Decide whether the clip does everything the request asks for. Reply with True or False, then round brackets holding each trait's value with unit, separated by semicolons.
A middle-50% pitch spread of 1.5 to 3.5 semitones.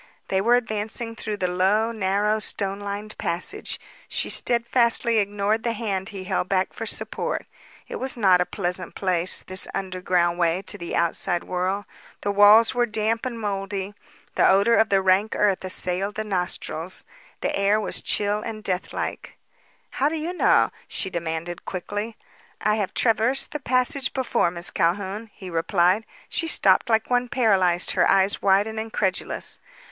True (3.1 semitones)